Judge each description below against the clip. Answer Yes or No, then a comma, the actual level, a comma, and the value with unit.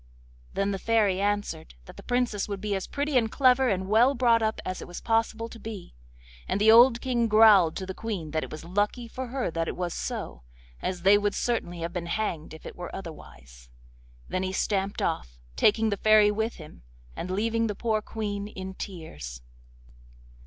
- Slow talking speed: No, average, 200 wpm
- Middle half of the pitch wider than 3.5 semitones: Yes, average, 4.1 semitones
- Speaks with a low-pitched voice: No, high, 205 Hz